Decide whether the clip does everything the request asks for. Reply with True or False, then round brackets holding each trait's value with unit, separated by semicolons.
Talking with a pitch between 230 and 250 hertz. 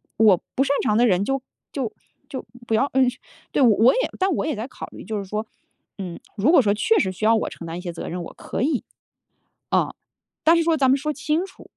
True (235 Hz)